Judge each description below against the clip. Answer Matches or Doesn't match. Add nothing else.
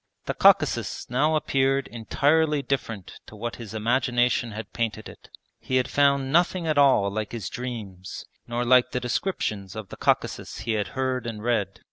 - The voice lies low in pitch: Matches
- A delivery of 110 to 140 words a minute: Doesn't match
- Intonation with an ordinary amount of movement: Matches